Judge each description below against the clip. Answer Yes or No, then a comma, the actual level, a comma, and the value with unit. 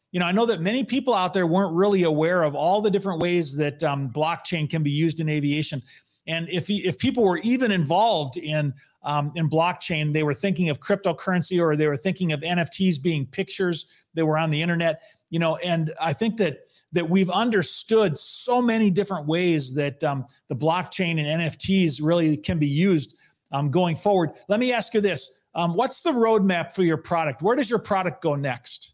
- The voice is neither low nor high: Yes, medium, 170 Hz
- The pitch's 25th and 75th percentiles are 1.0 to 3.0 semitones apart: No, average, 4.0 semitones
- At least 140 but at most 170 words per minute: No, fast, 205 wpm